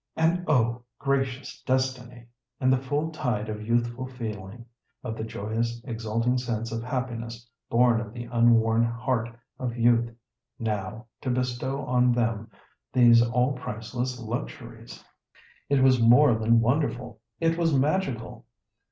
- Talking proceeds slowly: Yes, slow, 130 wpm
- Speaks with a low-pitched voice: Yes, low, 120 Hz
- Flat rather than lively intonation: Yes, narrow, 1.9 semitones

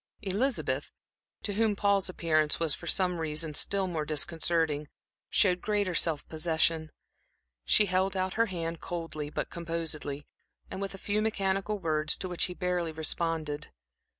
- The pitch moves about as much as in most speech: Yes, average, 3.4 semitones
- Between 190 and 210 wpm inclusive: No, average, 145 wpm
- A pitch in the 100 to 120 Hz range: No, medium, 170 Hz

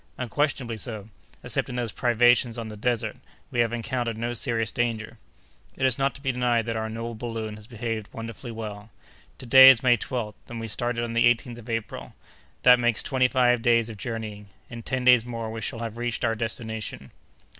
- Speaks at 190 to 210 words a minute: Yes, average, 200 wpm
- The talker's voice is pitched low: Yes, low, 115 Hz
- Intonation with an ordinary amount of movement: No, narrow, 1.6 semitones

